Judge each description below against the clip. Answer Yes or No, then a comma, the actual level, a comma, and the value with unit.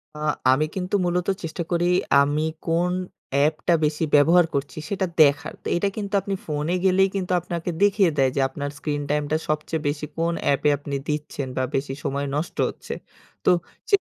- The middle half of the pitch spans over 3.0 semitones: Yes, average, 3.4 semitones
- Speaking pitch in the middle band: Yes, medium, 155 Hz